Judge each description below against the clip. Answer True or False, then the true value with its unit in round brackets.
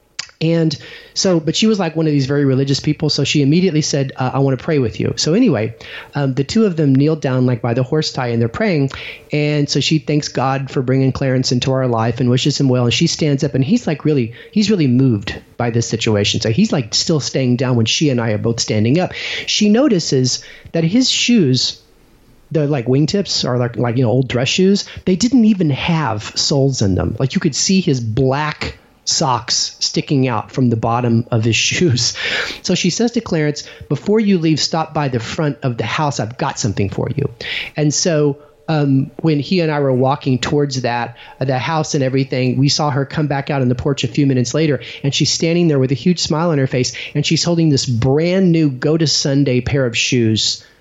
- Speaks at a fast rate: True (225 wpm)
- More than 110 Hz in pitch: True (140 Hz)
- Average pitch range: True (4.1 semitones)